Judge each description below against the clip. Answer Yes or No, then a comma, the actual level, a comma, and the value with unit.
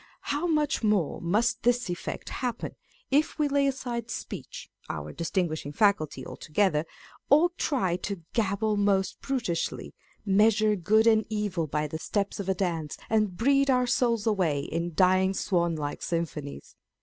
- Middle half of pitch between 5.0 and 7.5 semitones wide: Yes, wide, 5.6 semitones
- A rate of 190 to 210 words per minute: No, average, 150 wpm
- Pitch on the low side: No, high, 200 Hz